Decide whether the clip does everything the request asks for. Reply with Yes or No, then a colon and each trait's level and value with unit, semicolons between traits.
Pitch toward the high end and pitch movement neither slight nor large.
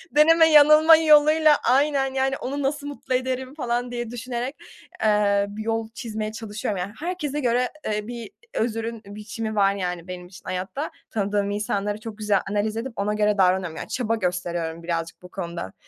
Yes: high, 220 Hz; average, 4.7 semitones